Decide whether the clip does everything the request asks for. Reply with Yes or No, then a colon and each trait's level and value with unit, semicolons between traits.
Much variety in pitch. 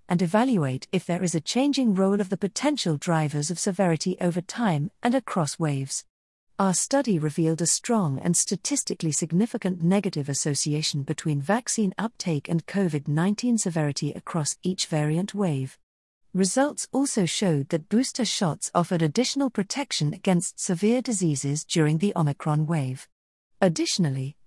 No: average, 4.9 semitones